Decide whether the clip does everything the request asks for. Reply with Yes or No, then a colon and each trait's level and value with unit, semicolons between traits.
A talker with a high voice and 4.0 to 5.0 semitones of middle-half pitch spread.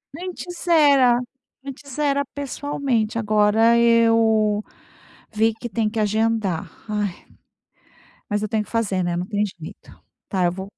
No: high, 225 Hz; average, 3.2 semitones